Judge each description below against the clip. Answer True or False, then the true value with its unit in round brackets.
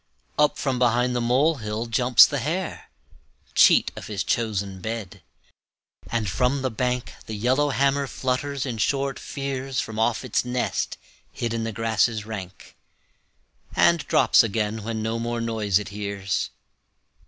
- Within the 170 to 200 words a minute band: False (140 wpm)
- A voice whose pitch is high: False (115 Hz)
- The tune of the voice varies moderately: True (3.2 semitones)